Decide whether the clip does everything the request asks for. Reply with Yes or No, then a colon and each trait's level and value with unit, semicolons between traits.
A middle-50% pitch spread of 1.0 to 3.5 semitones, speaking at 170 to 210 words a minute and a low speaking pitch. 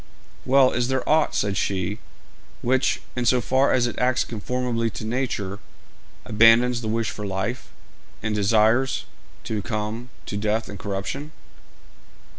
No: average, 3.2 semitones; average, 140 wpm; low, 115 Hz